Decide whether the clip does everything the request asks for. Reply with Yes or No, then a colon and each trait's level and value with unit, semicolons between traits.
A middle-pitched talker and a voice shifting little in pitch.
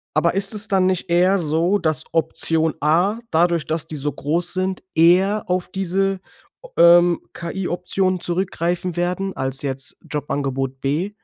No: medium, 175 Hz; average, 3.1 semitones